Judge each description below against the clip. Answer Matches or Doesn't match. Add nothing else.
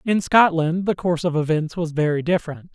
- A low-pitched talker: Doesn't match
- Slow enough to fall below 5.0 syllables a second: Doesn't match